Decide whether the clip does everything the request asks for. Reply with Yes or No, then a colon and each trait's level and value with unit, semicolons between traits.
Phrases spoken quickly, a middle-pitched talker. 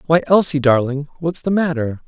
No: average, 175 wpm; medium, 150 Hz